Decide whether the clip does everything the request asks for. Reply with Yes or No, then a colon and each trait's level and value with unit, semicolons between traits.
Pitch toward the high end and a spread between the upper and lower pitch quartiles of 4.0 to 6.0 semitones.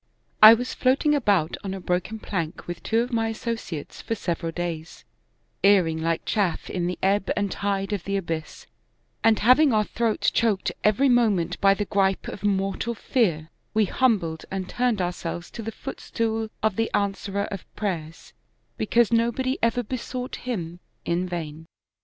Yes: high, 200 Hz; average, 4.4 semitones